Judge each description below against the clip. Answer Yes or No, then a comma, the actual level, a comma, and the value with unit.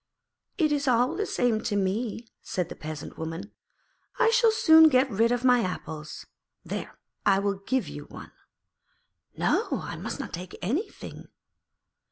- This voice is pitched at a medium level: No, high, 230 Hz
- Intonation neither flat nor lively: No, wide, 7.4 semitones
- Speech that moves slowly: No, average, 155 wpm